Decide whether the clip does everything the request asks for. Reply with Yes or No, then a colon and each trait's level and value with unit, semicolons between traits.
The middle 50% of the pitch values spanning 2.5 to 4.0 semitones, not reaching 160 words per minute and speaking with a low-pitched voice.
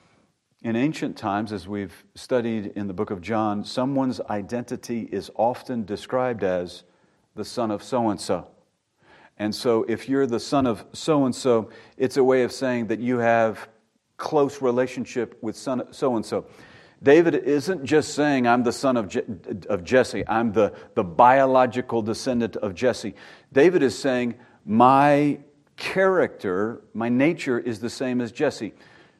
Yes: average, 2.9 semitones; average, 150 wpm; low, 120 Hz